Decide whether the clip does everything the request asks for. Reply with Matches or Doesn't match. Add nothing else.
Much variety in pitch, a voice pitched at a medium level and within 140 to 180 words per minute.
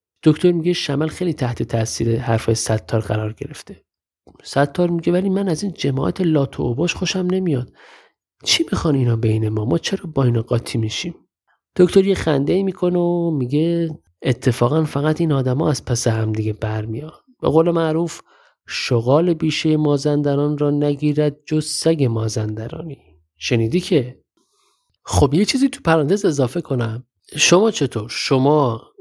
Matches